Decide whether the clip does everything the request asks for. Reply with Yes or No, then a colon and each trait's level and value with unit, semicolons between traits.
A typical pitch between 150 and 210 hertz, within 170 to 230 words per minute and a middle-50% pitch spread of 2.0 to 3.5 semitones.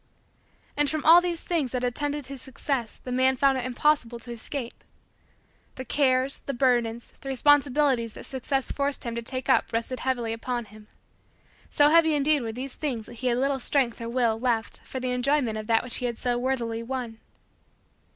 No: very high, 255 Hz; average, 190 wpm; average, 2.8 semitones